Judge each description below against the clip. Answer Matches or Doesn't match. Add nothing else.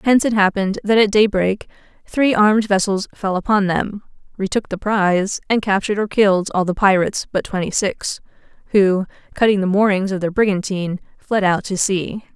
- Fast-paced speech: Doesn't match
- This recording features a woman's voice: Matches